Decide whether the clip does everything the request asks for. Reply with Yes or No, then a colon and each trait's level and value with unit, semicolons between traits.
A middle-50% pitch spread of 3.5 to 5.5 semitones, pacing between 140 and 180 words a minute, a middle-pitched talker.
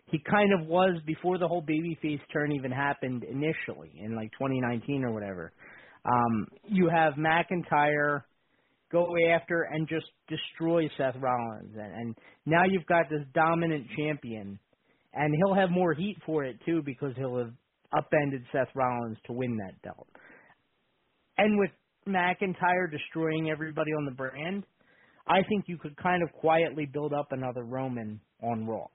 Yes: average, 4.9 semitones; average, 155 wpm; medium, 155 Hz